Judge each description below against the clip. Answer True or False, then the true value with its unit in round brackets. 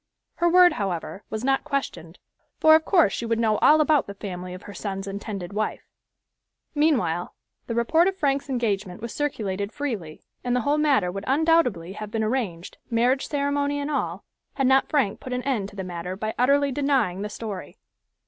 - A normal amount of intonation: False (6.3 semitones)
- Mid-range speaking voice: False (235 Hz)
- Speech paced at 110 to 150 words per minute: False (185 wpm)